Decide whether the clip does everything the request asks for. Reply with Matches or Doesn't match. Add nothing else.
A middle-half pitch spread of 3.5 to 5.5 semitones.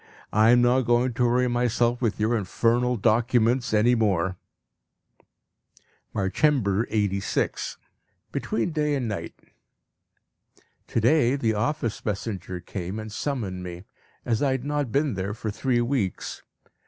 Doesn't match